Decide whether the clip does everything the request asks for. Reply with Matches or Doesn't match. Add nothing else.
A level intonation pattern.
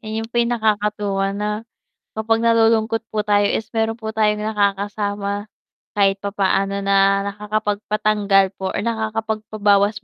Matches